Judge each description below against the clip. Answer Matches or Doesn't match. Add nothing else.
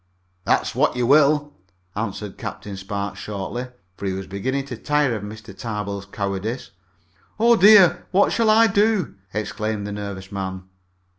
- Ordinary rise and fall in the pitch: Doesn't match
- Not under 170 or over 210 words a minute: Doesn't match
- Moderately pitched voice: Doesn't match